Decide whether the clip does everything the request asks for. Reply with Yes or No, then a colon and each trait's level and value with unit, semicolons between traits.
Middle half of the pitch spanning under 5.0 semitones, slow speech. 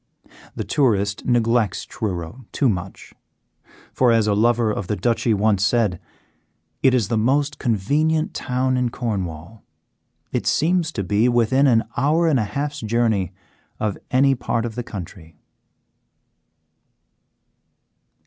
Yes: average, 4.0 semitones; slow, 130 wpm